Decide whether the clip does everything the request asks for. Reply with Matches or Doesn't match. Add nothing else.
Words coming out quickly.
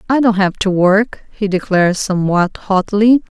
Doesn't match